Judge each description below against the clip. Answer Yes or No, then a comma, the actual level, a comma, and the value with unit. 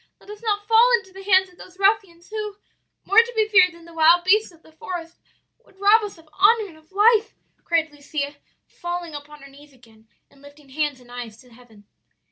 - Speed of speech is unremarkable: No, fast, 215 wpm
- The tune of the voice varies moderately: No, wide, 5.8 semitones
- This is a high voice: Yes, very high, 345 Hz